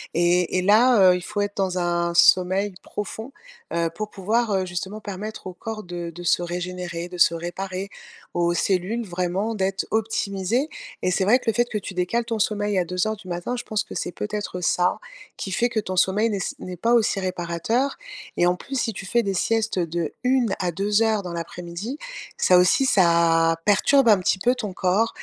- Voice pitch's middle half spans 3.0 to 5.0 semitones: Yes, average, 3.6 semitones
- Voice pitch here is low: No, high, 190 Hz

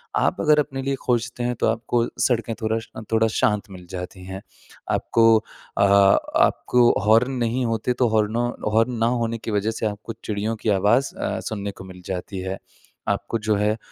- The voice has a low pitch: Yes, low, 110 Hz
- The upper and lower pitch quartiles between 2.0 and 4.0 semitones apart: Yes, narrow, 2.6 semitones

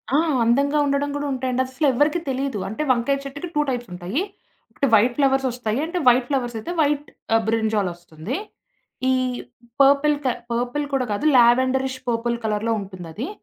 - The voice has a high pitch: Yes, very high, 255 Hz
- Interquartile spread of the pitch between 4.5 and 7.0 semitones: No, average, 3.5 semitones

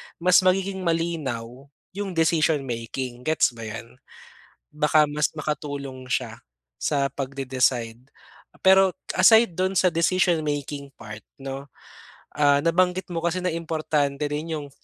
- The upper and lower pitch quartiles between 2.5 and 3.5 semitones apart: No, average, 4.2 semitones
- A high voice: No, medium, 150 Hz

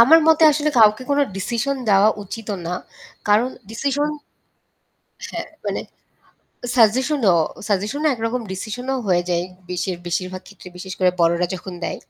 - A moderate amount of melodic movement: No, wide, 5.9 semitones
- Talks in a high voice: Yes, high, 215 Hz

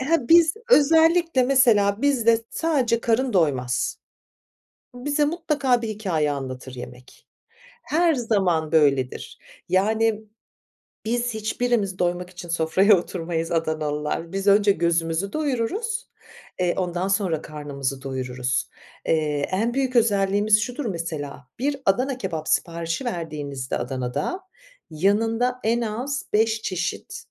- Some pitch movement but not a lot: No, wide, 7.3 semitones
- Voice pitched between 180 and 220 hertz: Yes, high, 200 Hz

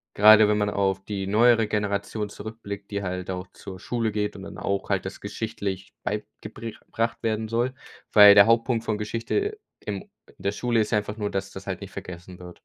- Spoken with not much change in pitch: Yes, narrow, 2.2 semitones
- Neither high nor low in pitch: No, low, 105 Hz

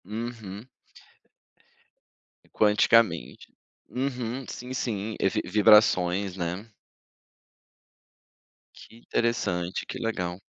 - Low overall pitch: Yes, low, 105 Hz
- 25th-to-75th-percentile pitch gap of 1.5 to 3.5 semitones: No, average, 3.9 semitones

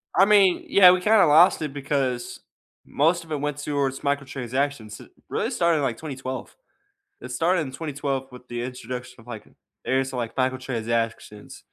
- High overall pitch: No, low, 135 Hz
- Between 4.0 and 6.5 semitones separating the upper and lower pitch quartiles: No, average, 3.3 semitones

